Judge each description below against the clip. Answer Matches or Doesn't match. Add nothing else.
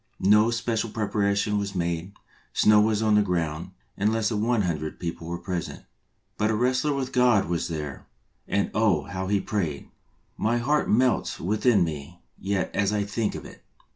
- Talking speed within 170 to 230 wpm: Matches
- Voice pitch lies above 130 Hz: Doesn't match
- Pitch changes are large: Doesn't match